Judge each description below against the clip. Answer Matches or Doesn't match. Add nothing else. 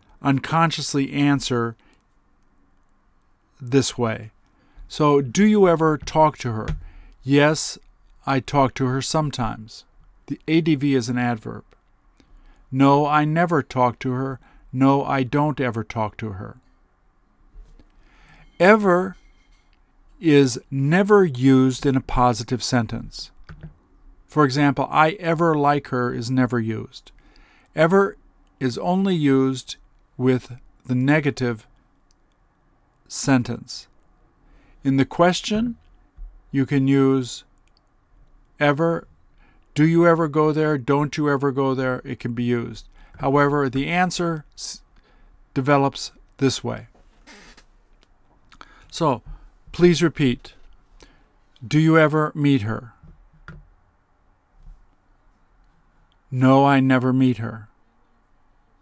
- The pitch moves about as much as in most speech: Matches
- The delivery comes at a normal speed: Doesn't match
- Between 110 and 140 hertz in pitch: Matches